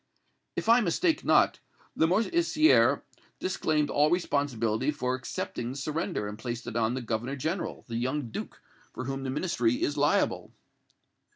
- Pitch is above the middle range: No, medium, 140 Hz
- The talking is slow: No, average, 150 wpm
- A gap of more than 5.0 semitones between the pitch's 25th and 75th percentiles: Yes, wide, 5.6 semitones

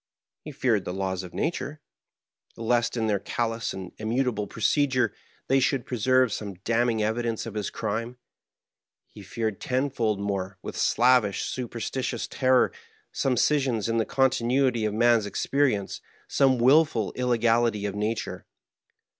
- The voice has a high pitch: No, low, 115 Hz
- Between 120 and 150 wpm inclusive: Yes, average, 140 wpm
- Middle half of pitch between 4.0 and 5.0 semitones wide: No, average, 3.2 semitones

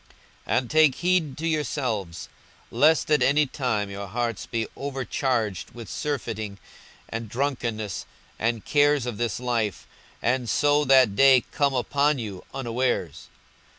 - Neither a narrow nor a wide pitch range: Yes, average, 4.5 semitones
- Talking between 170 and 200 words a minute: No, slow, 135 wpm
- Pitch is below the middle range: Yes, low, 125 Hz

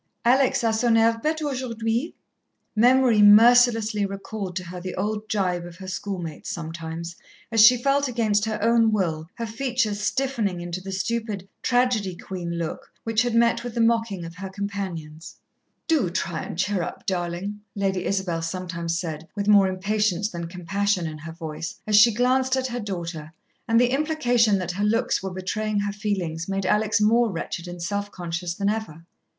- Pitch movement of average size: Yes, average, 4.5 semitones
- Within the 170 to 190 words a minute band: Yes, average, 175 wpm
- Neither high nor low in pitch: No, high, 205 Hz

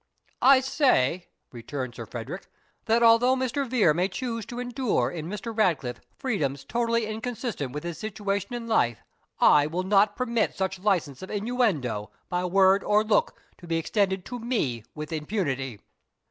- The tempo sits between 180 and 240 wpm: No, average, 160 wpm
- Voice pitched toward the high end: Yes, high, 200 Hz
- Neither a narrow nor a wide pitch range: No, wide, 6.9 semitones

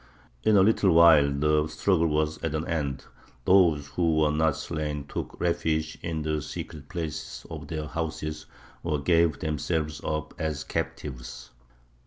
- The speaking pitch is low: Yes, very low, 80 Hz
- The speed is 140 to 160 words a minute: Yes, average, 150 wpm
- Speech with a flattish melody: Yes, narrow, 1.6 semitones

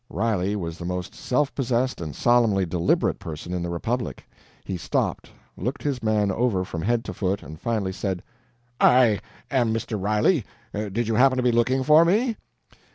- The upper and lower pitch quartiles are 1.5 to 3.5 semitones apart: No, average, 5.1 semitones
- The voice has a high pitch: No, low, 110 Hz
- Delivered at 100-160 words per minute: No, average, 175 wpm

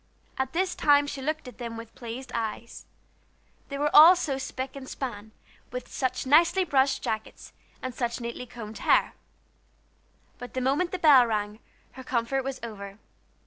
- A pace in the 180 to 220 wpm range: No, average, 165 wpm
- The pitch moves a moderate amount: Yes, average, 3.4 semitones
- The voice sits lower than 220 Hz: No, very high, 260 Hz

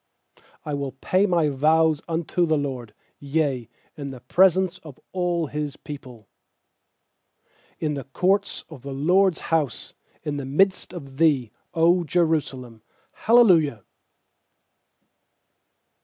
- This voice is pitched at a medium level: Yes, medium, 150 Hz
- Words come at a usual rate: No, slow, 115 wpm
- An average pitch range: Yes, average, 4.2 semitones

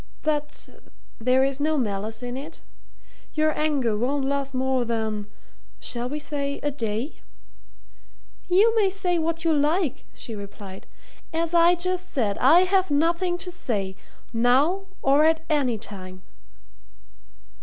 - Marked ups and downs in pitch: Yes, wide, 5.8 semitones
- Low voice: No, very high, 285 Hz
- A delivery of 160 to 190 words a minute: No, slow, 135 wpm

